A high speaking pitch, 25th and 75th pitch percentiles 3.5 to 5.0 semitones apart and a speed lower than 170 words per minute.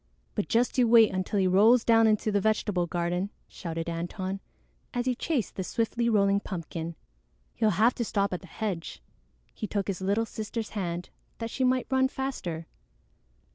No: high, 205 Hz; average, 4.0 semitones; average, 175 wpm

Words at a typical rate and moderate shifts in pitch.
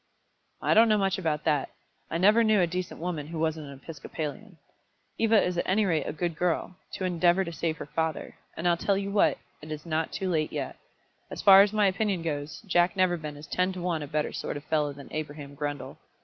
No: fast, 225 wpm; average, 3.7 semitones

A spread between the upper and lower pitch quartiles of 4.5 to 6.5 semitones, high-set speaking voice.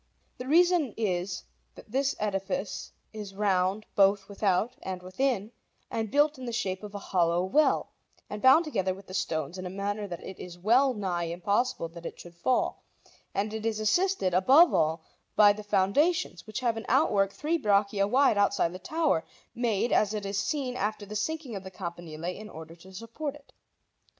Yes: average, 4.8 semitones; high, 205 Hz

